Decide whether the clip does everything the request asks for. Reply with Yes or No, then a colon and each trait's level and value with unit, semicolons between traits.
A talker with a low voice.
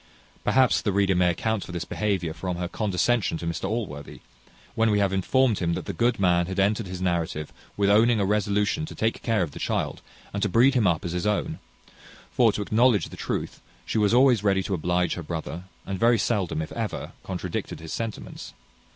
Yes: low, 100 Hz